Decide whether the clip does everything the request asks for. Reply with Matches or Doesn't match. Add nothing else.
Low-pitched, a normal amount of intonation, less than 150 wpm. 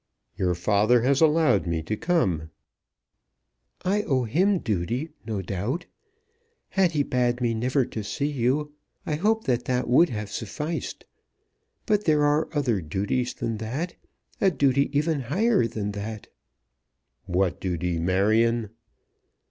Doesn't match